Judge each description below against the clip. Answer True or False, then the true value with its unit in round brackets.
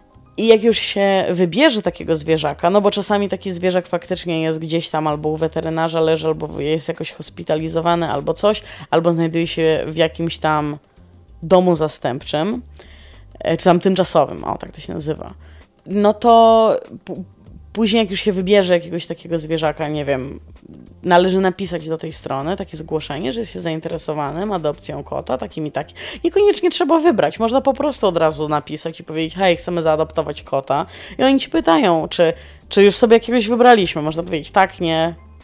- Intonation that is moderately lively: True (4.1 semitones)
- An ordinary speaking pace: False (170 wpm)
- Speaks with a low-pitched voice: False (165 Hz)